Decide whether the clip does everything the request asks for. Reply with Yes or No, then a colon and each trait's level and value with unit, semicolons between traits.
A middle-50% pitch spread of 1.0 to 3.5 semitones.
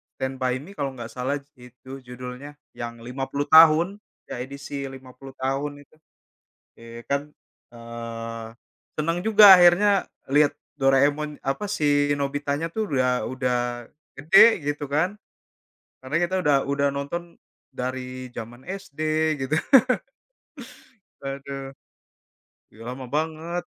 Yes: average, 3.2 semitones